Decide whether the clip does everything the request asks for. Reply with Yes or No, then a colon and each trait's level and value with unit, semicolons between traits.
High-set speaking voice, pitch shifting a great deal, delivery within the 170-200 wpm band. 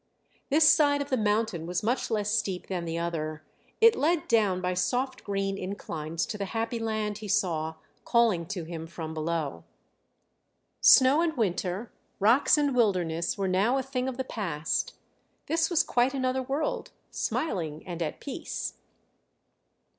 No: high, 210 Hz; wide, 7.0 semitones; average, 155 wpm